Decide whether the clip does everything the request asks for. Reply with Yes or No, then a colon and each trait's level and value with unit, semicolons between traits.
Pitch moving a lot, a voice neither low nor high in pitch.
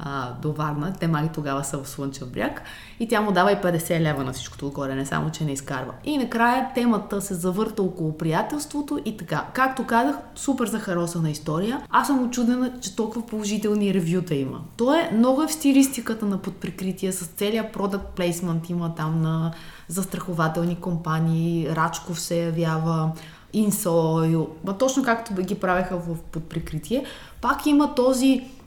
Yes: wide, 6.1 semitones; medium, 180 Hz